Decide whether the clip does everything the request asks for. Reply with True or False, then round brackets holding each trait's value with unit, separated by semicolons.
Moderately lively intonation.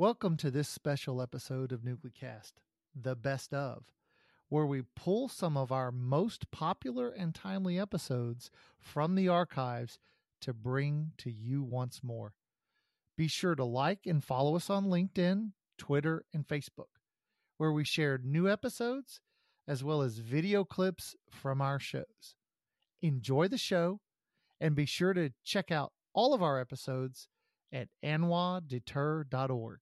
False (5.8 semitones)